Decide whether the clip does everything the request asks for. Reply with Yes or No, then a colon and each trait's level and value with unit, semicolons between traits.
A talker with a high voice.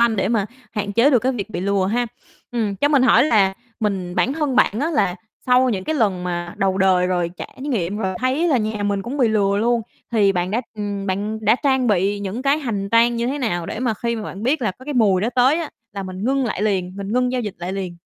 Yes: high, 215 Hz